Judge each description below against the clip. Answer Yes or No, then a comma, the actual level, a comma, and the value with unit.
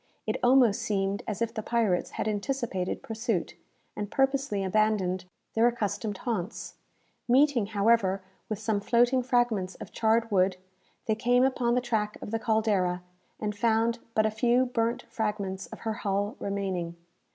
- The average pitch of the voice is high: Yes, high, 220 Hz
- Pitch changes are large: No, average, 3.0 semitones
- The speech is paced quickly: No, average, 150 wpm